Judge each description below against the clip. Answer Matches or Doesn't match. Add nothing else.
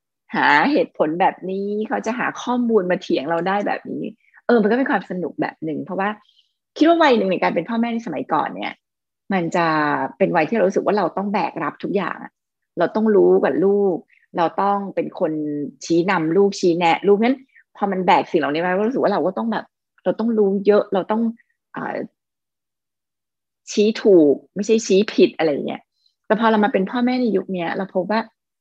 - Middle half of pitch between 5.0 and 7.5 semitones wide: Doesn't match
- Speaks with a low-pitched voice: Doesn't match